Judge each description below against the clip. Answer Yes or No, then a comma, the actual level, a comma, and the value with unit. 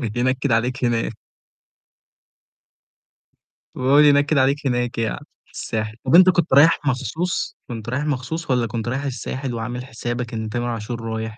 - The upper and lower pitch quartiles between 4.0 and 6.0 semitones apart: No, average, 3.5 semitones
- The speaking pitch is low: Yes, low, 125 Hz